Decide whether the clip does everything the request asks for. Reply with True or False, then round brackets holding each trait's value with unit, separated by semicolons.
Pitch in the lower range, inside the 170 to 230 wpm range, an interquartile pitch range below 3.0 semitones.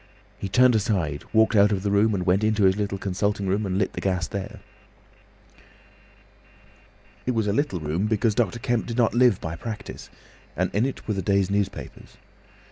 True (100 Hz; 190 wpm; 2.5 semitones)